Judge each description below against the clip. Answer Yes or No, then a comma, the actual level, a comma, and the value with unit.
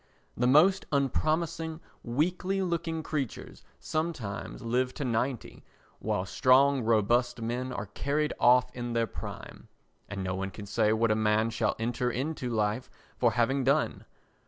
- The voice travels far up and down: No, average, 4.9 semitones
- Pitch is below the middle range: Yes, low, 125 Hz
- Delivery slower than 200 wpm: Yes, average, 145 wpm